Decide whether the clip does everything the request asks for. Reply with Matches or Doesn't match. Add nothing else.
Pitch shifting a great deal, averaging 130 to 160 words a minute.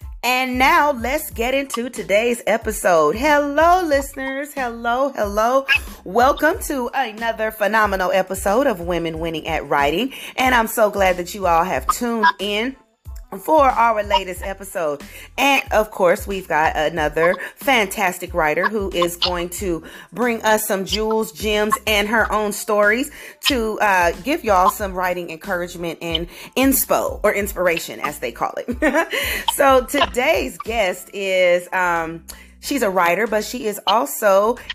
Matches